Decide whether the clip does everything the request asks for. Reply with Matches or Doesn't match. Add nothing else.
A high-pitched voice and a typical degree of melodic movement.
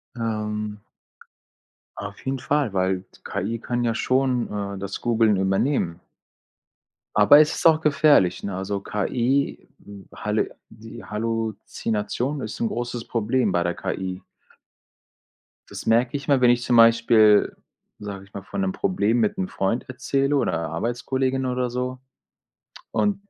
Doesn't match